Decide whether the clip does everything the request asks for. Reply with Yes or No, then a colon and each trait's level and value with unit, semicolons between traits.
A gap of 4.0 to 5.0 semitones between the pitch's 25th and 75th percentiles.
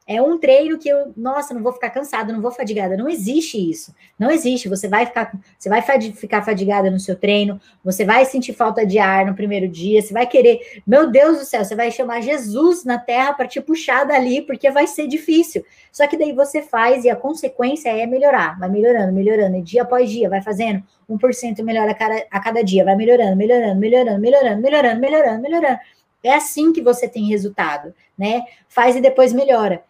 Yes: average, 4.4 semitones